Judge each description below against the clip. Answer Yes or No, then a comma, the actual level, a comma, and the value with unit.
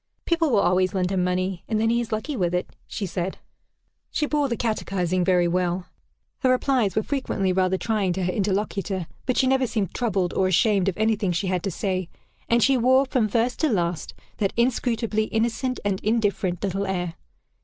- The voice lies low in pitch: No, high, 200 Hz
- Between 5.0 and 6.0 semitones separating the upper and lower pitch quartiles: No, average, 4.2 semitones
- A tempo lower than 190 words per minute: No, average, 195 wpm